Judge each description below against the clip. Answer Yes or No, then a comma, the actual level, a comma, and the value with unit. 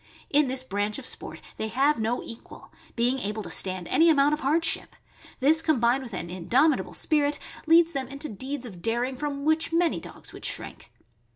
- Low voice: No, very high, 265 Hz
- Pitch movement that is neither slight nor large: Yes, average, 4.8 semitones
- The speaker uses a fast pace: No, average, 185 wpm